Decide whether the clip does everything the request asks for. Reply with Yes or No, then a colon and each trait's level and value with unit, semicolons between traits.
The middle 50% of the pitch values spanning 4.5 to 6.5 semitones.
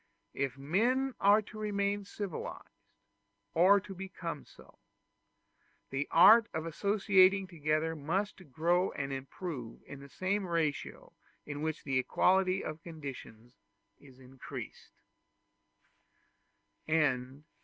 Yes: wide, 5.6 semitones